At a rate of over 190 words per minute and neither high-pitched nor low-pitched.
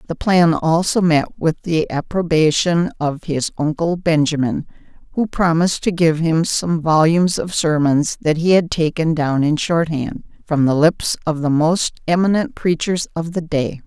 No: average, 170 wpm; medium, 160 Hz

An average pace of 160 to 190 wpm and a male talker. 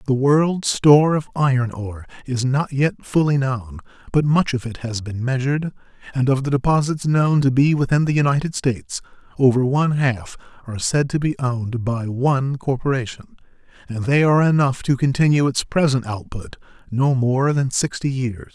Yes: average, 175 wpm; male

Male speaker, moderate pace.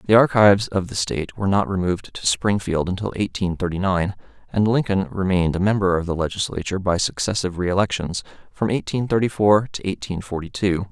Yes: male; average, 180 wpm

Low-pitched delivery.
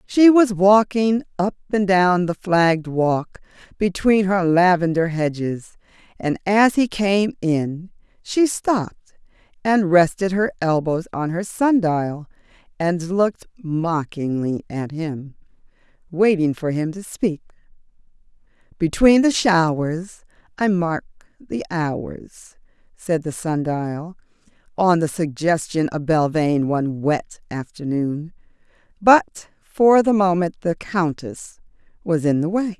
No: medium, 175 Hz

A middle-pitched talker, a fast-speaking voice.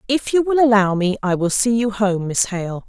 No: high, 215 Hz; fast, 250 wpm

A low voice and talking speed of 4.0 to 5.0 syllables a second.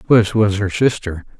Yes: low, 105 Hz; 4.5 syllables/s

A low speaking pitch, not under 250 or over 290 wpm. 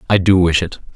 Yes: very low, 90 Hz; fast, 255 wpm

